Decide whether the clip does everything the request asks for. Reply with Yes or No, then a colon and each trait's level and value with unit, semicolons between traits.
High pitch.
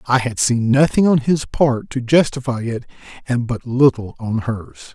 No: low, 125 Hz